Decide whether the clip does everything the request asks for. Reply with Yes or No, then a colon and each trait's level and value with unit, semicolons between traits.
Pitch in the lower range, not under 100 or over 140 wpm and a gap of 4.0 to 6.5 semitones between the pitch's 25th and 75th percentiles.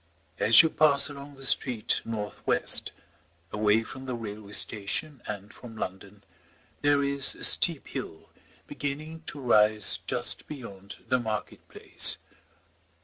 Yes: low, 115 Hz; slow, 135 wpm; average, 5.0 semitones